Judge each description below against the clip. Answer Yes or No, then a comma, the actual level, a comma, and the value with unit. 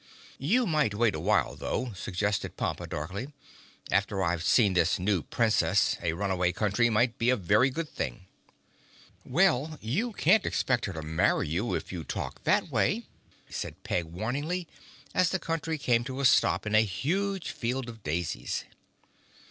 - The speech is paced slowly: No, average, 165 wpm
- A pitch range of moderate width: No, wide, 7.6 semitones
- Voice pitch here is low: Yes, low, 115 Hz